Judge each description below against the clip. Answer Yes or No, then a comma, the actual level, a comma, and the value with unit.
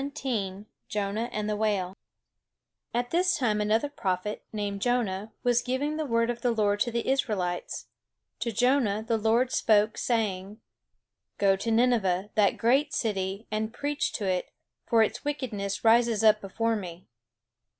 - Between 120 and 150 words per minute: No, average, 160 wpm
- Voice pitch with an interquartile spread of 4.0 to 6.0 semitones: No, average, 3.1 semitones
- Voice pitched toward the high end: Yes, high, 220 Hz